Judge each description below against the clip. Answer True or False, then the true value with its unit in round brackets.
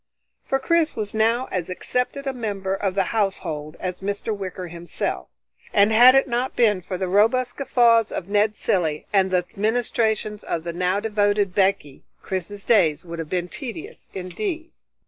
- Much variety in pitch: False (4.2 semitones)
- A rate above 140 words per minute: True (165 wpm)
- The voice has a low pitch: False (205 Hz)